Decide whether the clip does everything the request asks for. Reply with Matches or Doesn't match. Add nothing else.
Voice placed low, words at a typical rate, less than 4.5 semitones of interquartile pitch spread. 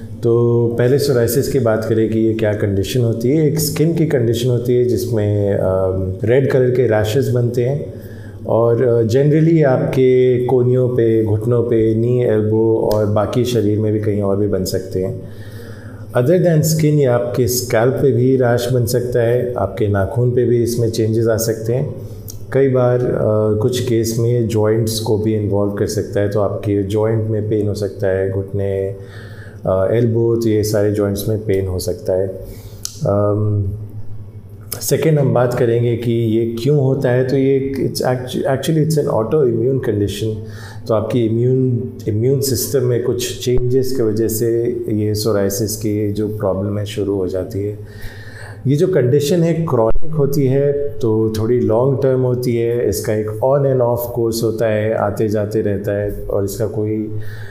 Matches